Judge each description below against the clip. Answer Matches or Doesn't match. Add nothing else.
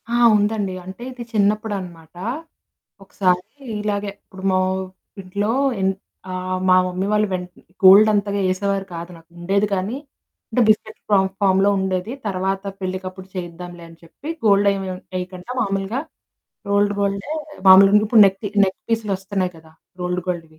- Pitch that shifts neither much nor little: Doesn't match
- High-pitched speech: Matches